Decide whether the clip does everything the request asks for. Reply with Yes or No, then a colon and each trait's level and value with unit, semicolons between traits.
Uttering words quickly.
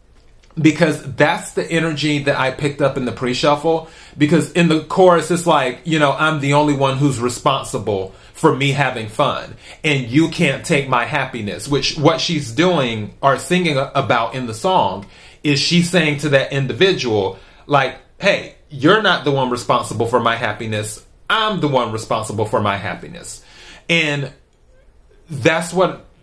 No: average, 165 wpm